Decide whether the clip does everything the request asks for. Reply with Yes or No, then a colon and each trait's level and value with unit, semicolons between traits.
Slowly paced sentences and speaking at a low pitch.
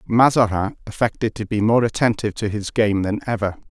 No: average, 180 wpm; low, 110 Hz